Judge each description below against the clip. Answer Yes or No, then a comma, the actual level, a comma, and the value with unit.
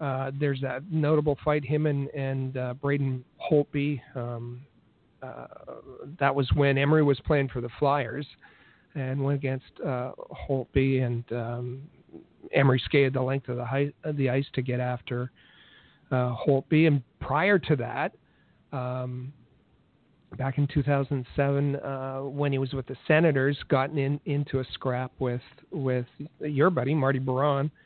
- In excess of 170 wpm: No, average, 150 wpm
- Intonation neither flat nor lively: No, narrow, 2.0 semitones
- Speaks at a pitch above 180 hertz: No, low, 135 Hz